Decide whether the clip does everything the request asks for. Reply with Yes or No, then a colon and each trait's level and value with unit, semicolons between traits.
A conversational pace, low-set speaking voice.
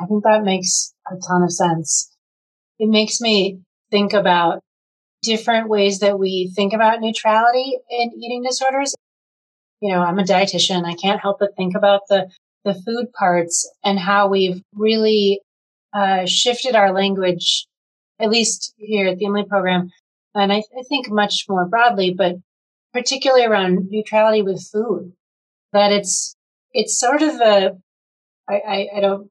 No: average, 160 wpm; high, 200 Hz